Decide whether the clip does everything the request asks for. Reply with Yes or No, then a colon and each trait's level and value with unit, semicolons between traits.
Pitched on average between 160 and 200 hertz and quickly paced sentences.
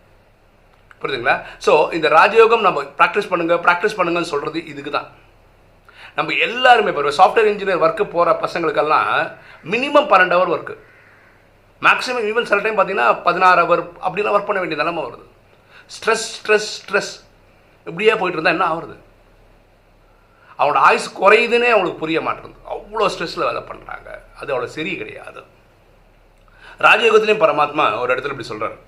Yes: medium, 185 Hz; fast, 135 wpm